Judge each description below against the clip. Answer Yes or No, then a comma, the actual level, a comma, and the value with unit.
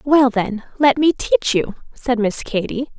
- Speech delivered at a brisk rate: No, average, 180 wpm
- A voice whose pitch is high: Yes, very high, 255 Hz